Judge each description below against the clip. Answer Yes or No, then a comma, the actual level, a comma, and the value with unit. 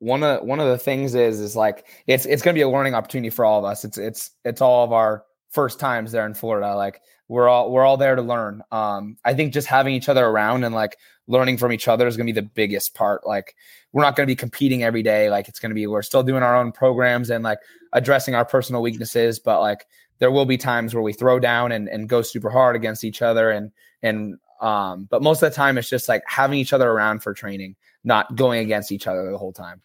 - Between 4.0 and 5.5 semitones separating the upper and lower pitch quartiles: No, average, 3.2 semitones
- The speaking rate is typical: No, fast, 260 wpm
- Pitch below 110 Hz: No, low, 120 Hz